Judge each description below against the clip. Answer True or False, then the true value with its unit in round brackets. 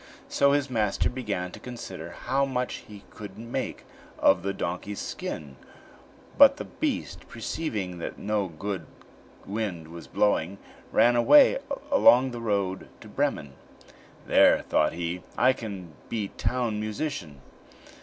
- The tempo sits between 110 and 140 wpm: True (135 wpm)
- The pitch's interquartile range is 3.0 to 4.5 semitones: False (5.1 semitones)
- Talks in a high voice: False (105 Hz)